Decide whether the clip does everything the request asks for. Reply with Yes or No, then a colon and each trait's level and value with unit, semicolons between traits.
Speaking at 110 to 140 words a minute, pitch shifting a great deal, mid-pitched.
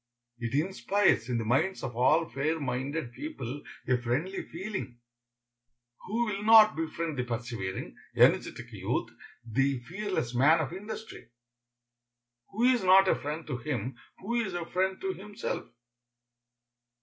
Yes: slow, 135 wpm; wide, 7.5 semitones; medium, 160 Hz